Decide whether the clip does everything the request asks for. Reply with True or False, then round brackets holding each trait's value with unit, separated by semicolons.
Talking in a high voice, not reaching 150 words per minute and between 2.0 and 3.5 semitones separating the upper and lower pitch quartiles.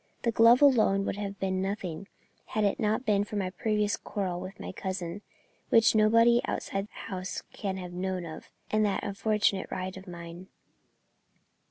False (195 Hz; 175 wpm; 2.4 semitones)